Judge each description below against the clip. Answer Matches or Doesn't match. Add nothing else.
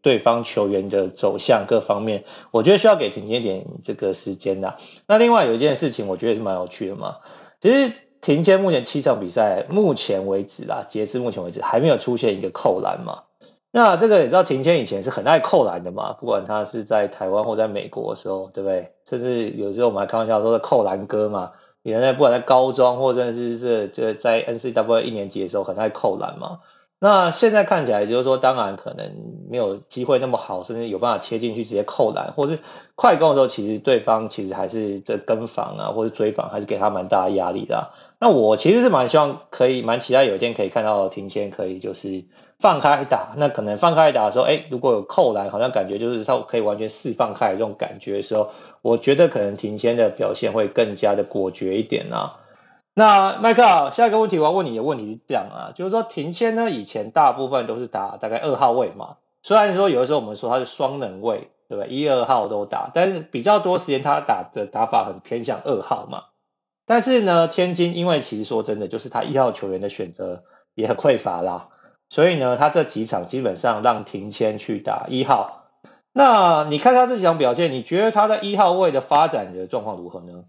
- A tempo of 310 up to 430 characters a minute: Matches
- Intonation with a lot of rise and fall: Matches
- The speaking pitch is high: Doesn't match